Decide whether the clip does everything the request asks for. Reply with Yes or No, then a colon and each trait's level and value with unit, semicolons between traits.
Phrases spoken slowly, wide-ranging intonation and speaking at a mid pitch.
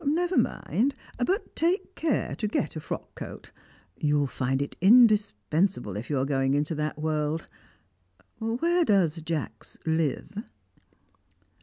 Yes: slow, 130 wpm; wide, 8.0 semitones; medium, 160 Hz